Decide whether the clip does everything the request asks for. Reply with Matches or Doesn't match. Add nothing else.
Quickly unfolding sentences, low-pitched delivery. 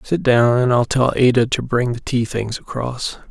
Matches